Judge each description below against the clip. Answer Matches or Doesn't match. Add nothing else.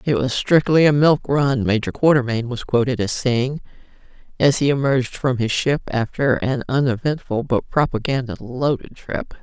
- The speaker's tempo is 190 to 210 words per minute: Doesn't match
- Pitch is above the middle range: Doesn't match